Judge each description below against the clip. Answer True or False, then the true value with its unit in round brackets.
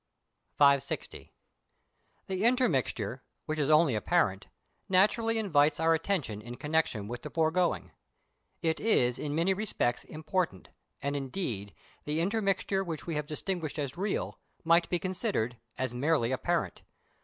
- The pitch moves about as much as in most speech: False (6.0 semitones)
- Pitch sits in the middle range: True (160 Hz)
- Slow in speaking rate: True (130 wpm)